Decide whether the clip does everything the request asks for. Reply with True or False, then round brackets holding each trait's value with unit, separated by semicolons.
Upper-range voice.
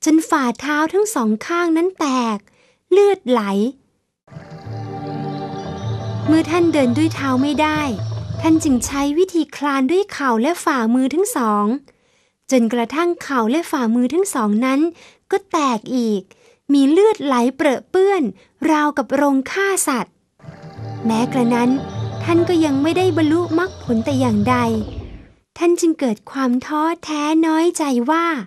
True (280 Hz)